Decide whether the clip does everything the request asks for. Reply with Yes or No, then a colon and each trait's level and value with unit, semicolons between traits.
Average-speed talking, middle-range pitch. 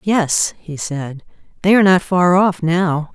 Yes: average, 170 wpm; medium, 175 Hz